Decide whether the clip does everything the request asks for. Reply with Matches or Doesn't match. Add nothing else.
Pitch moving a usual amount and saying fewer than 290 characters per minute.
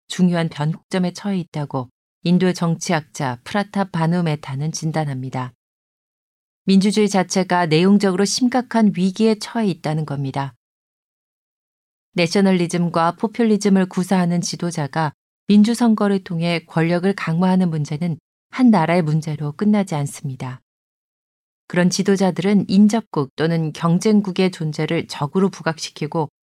Doesn't match